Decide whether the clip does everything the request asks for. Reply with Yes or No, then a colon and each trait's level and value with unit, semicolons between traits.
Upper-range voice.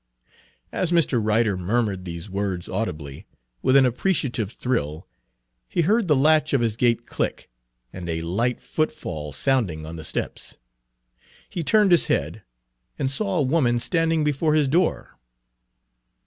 No: low, 120 Hz